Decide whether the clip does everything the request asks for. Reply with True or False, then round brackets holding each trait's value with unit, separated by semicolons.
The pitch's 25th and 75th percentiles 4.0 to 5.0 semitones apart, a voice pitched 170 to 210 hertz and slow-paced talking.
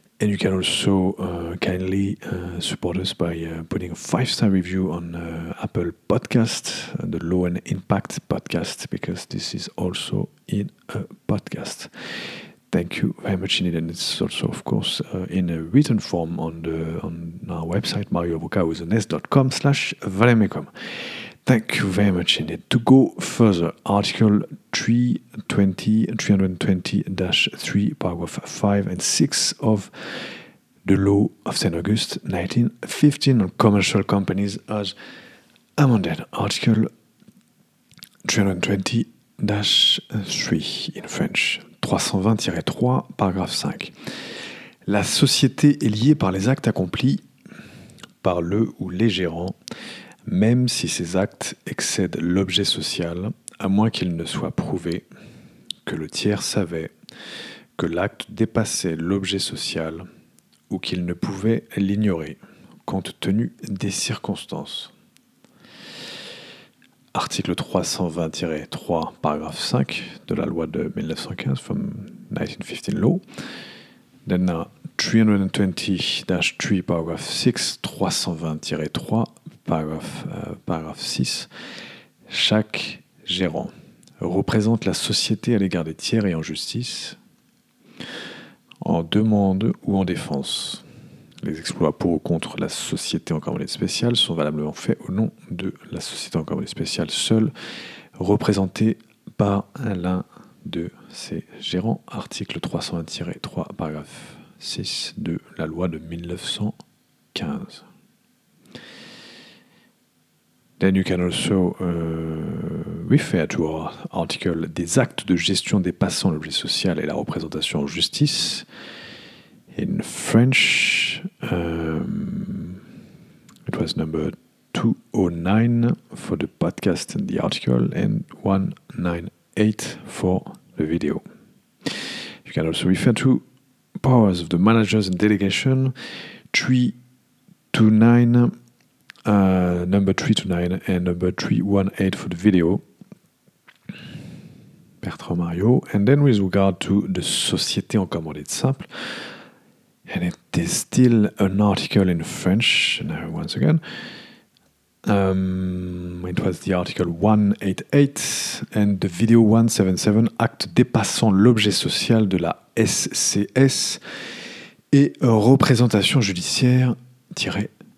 False (4.3 semitones; 100 Hz; 115 wpm)